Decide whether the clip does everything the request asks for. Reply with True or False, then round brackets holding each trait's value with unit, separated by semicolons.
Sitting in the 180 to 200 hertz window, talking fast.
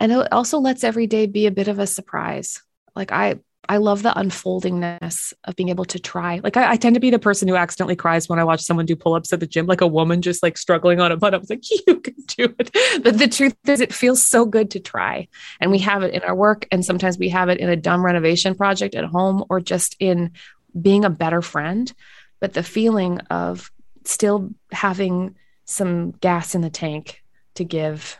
True (185 Hz; 230 wpm)